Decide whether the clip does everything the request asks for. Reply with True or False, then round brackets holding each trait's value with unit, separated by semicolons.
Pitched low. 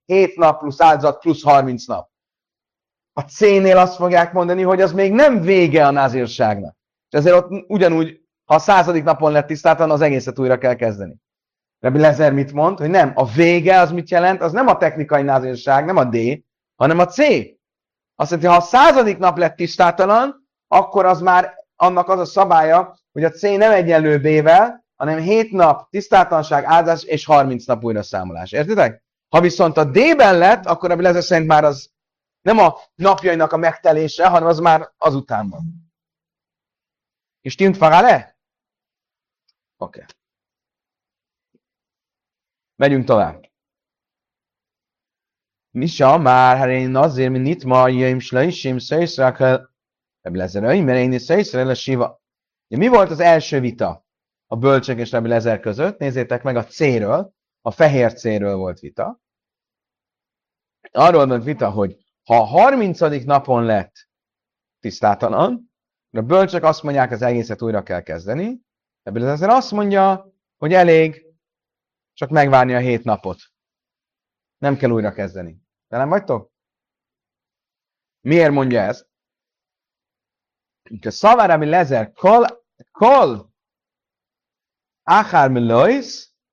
False (155 Hz)